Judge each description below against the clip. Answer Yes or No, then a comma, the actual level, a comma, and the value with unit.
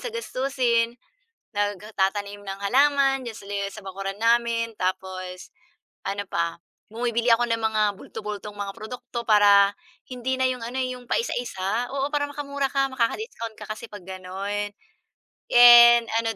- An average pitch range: Yes, average, 3.7 semitones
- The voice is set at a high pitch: Yes, high, 230 Hz